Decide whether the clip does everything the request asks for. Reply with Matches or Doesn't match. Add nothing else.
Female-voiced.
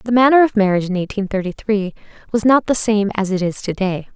Matches